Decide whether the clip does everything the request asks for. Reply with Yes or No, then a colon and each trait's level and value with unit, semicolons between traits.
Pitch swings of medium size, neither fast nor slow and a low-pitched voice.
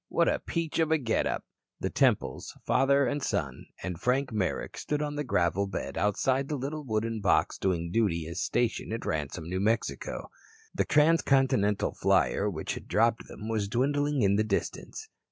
No: wide, 6.0 semitones; average, 175 wpm; low, 115 Hz